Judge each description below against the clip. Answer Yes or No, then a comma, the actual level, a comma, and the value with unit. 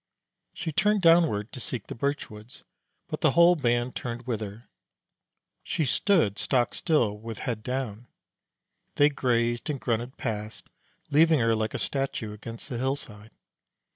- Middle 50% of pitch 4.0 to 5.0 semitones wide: Yes, average, 4.4 semitones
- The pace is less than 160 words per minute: Yes, average, 150 wpm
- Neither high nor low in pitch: No, low, 120 Hz